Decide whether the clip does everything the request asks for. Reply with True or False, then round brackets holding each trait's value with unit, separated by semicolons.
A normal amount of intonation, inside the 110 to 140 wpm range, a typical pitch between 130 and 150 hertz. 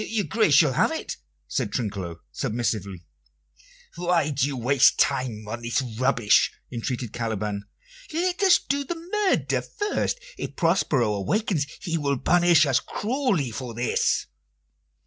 False (8.5 semitones; 135 wpm; 135 Hz)